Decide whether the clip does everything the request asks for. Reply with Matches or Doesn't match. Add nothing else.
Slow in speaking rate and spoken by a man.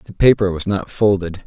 Doesn't match